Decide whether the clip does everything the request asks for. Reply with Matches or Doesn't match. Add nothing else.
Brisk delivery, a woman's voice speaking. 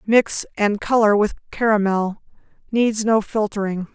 Doesn't match